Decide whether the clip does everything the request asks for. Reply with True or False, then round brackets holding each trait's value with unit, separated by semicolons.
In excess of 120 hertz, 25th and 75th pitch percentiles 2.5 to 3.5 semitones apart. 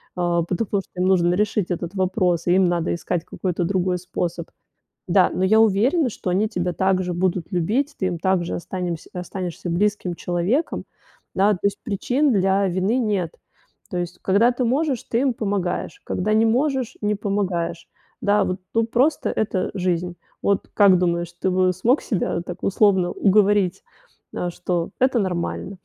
True (190 Hz; 3.1 semitones)